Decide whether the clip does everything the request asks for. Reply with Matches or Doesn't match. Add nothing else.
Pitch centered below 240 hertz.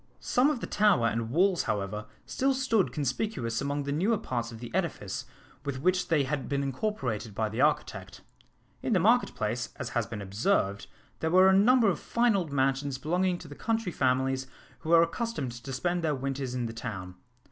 Matches